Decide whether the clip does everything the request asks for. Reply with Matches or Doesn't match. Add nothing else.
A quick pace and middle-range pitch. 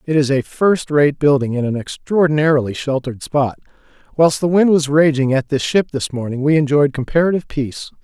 Doesn't match